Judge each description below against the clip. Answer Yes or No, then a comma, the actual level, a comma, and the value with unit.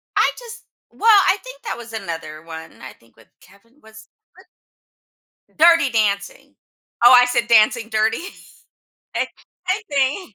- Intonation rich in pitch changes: Yes, wide, 6.4 semitones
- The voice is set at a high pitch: Yes, high, 230 Hz